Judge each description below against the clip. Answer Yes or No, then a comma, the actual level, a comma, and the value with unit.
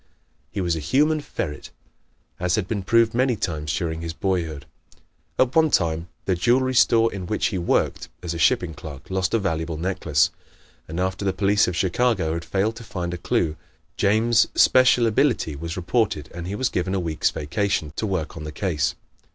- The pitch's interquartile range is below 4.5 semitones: No, average, 5.1 semitones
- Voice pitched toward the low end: Yes, very low, 95 Hz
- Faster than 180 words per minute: Yes, average, 190 wpm